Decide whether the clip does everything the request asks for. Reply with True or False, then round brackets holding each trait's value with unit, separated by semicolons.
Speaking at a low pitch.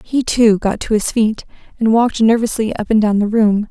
False (220 Hz)